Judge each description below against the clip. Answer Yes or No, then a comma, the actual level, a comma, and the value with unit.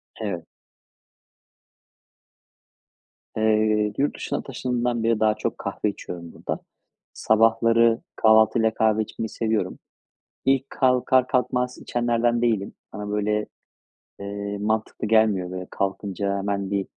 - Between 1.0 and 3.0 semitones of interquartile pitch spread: Yes, narrow, 2.4 semitones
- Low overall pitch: Yes, low, 110 Hz